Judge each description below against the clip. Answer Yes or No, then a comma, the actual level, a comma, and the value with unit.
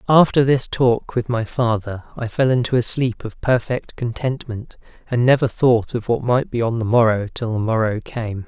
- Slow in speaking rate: No, average, 200 wpm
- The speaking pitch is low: Yes, low, 120 Hz